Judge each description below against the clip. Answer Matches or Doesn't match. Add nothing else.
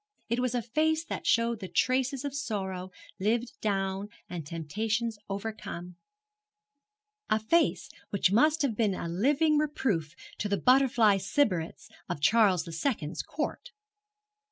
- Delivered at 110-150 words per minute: Matches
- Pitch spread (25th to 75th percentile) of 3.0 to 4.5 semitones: Doesn't match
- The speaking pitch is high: Matches